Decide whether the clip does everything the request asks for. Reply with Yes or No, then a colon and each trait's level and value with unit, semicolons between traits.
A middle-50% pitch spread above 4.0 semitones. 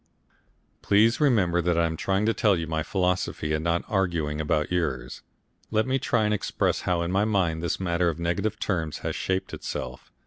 No: average, 3.6 semitones